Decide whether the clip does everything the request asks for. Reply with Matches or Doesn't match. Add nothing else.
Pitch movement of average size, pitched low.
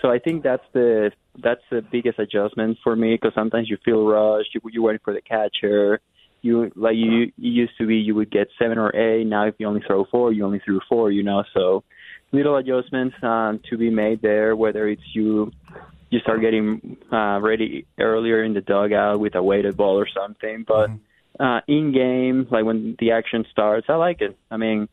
Doesn't match